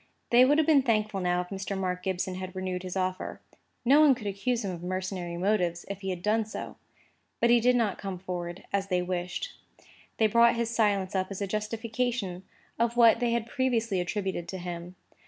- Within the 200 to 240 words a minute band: Yes, fast, 205 wpm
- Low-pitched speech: No, high, 195 Hz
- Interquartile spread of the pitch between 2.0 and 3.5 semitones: No, average, 4.1 semitones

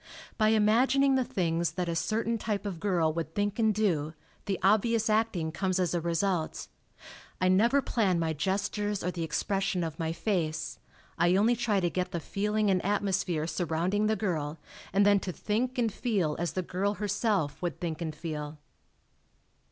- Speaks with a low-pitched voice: No, high, 190 Hz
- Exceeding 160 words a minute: Yes, average, 175 wpm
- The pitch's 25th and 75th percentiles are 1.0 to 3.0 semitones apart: No, average, 4.0 semitones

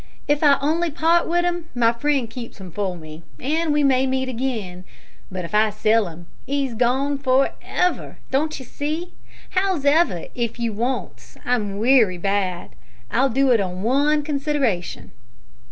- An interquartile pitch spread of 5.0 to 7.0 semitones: Yes, wide, 5.6 semitones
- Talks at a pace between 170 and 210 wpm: No, average, 160 wpm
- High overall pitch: Yes, very high, 260 Hz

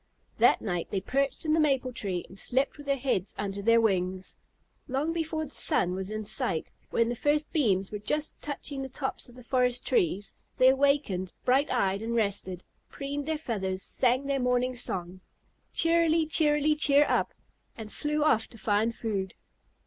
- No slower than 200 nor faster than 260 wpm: No, average, 180 wpm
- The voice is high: Yes, very high, 250 Hz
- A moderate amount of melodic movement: No, wide, 6.4 semitones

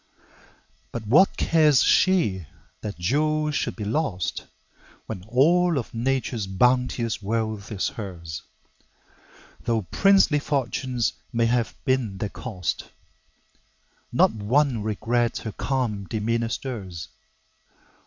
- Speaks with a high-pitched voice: No, low, 115 Hz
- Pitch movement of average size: Yes, average, 4.4 semitones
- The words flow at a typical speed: No, slow, 105 wpm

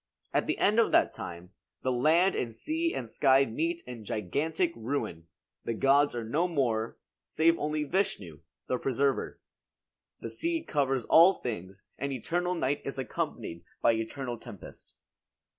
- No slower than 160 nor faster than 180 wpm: No, average, 150 wpm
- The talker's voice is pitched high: No, low, 135 Hz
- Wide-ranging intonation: Yes, wide, 6.2 semitones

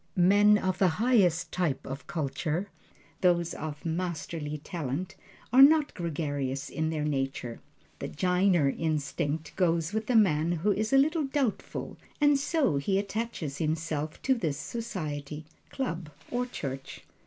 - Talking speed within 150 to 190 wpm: No, average, 140 wpm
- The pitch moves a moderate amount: No, wide, 5.7 semitones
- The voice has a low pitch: No, medium, 170 Hz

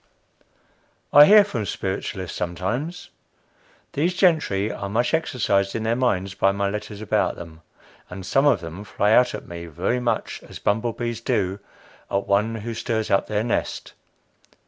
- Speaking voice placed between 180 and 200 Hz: No, low, 105 Hz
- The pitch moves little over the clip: No, average, 3.9 semitones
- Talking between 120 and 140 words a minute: No, average, 160 wpm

